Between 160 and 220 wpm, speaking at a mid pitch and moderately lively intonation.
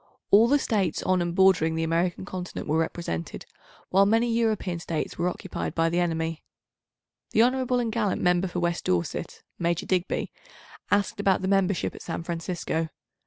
Yes: average, 165 wpm; medium, 180 Hz; average, 3.2 semitones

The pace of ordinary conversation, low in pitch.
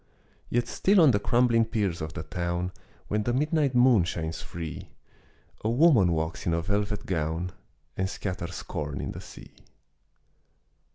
Yes: average, 155 wpm; very low, 95 Hz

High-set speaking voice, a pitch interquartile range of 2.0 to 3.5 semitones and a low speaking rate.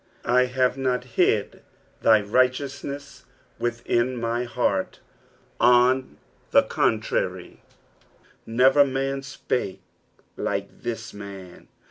No: low, 125 Hz; narrow, 2.5 semitones; slow, 95 wpm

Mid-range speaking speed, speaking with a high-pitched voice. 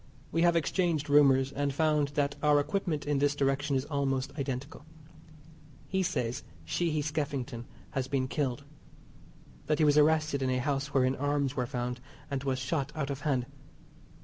No: average, 165 wpm; medium, 140 Hz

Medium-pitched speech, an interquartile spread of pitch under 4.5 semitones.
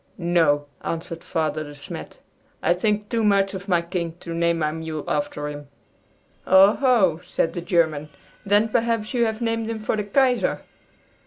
No: medium, 180 Hz; average, 4.9 semitones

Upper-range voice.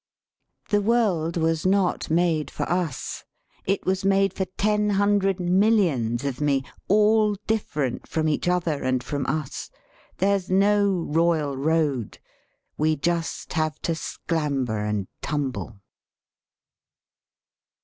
No: medium, 165 Hz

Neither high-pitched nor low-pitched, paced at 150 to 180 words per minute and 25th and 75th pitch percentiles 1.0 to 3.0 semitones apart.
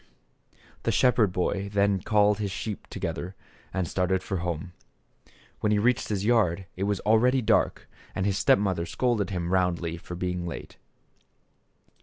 No: very low, 95 Hz; average, 160 wpm; average, 2.7 semitones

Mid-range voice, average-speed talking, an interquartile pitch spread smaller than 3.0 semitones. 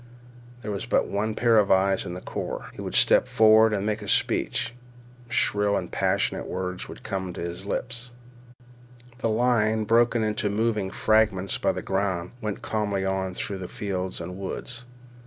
No: low, 105 Hz; average, 165 wpm; narrow, 2.5 semitones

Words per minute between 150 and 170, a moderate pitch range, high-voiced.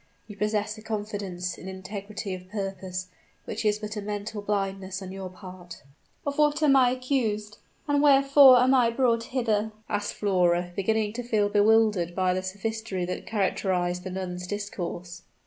Yes: average, 165 wpm; average, 3.1 semitones; high, 205 Hz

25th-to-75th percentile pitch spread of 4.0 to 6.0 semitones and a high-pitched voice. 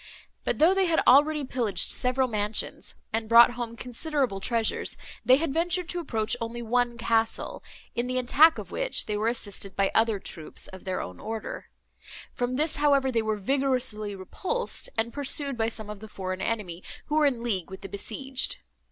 Yes: average, 4.6 semitones; high, 235 Hz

